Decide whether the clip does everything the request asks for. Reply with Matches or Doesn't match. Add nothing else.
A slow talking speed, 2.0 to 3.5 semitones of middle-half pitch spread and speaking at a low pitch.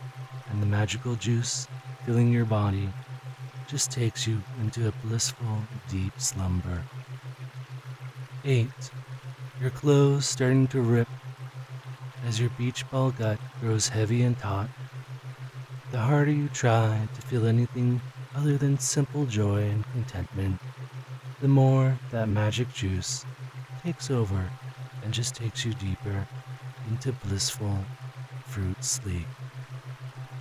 Matches